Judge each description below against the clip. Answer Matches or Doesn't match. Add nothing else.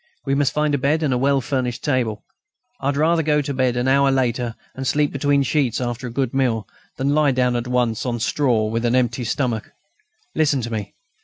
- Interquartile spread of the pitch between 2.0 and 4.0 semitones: Matches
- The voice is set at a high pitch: Doesn't match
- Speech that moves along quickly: Matches